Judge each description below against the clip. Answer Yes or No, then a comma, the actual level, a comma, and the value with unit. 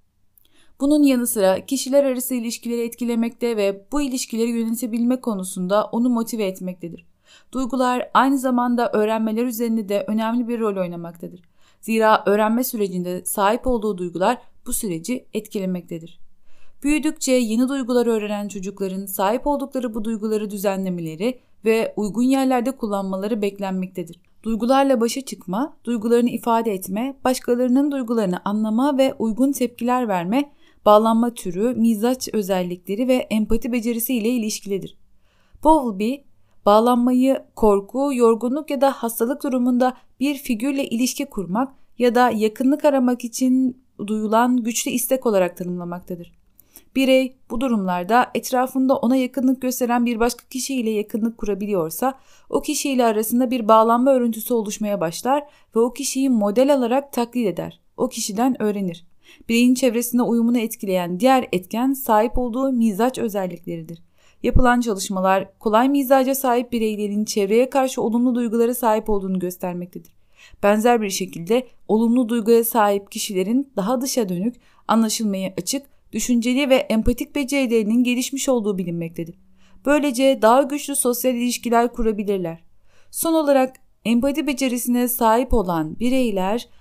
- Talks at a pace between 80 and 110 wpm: No, average, 125 wpm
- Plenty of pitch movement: No, average, 3.6 semitones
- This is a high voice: Yes, high, 235 Hz